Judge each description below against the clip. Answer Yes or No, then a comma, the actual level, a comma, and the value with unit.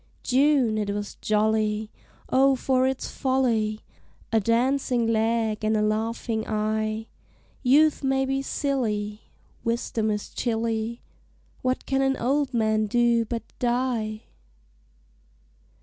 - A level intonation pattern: No, average, 3.2 semitones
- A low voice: No, high, 230 Hz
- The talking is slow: Yes, slow, 115 wpm